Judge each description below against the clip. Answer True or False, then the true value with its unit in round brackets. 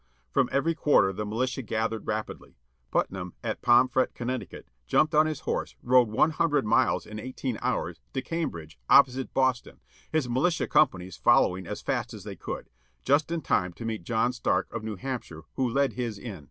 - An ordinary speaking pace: True (180 wpm)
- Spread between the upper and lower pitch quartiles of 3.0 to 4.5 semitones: True (4.1 semitones)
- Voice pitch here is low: True (125 Hz)